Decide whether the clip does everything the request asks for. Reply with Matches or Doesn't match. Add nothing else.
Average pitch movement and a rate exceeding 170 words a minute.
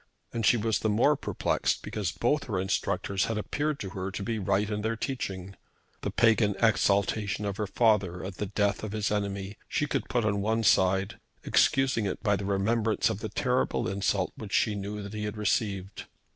Doesn't match